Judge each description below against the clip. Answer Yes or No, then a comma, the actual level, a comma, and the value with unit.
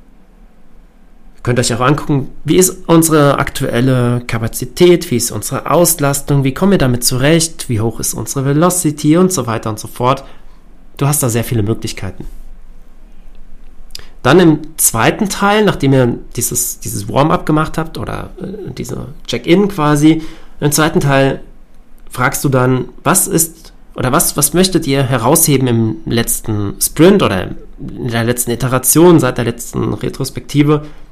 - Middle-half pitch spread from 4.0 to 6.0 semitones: Yes, average, 4.5 semitones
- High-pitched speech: No, low, 135 Hz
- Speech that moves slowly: No, average, 150 wpm